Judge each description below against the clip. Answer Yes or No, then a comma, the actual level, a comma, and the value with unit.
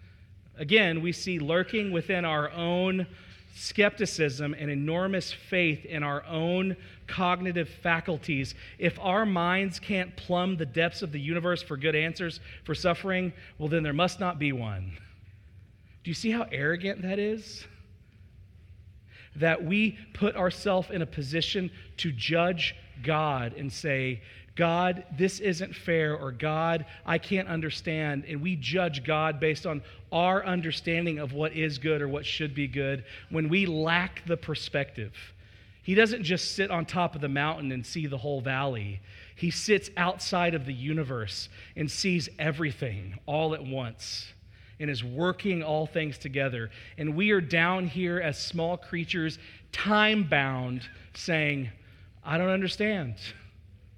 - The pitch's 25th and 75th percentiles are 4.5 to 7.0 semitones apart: Yes, wide, 5.4 semitones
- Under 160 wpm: Yes, average, 150 wpm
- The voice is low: No, medium, 155 Hz